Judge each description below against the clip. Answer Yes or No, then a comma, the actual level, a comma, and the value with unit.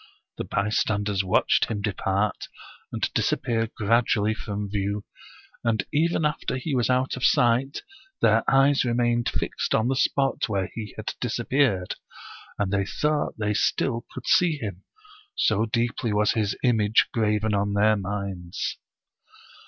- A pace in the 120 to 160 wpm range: Yes, average, 145 wpm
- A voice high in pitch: No, low, 110 Hz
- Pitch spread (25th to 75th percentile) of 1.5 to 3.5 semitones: Yes, average, 3.1 semitones